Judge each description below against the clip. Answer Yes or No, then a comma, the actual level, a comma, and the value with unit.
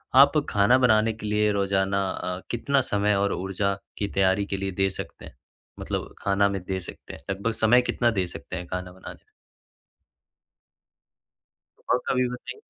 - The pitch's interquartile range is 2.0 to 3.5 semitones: Yes, narrow, 2.6 semitones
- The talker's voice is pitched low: Yes, low, 100 Hz